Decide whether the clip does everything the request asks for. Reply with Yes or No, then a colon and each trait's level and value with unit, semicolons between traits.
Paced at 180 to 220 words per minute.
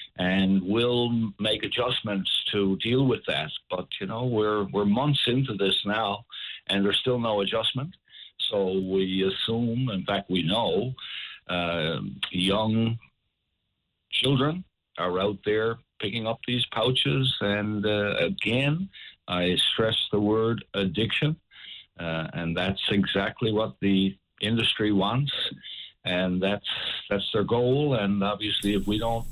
No: slow, 135 wpm